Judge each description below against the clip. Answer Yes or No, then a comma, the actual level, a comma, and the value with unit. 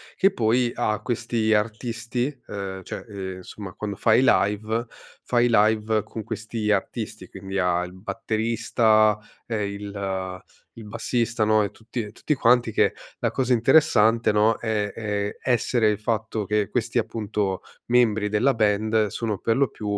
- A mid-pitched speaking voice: No, low, 110 Hz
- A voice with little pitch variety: Yes, narrow, 2.0 semitones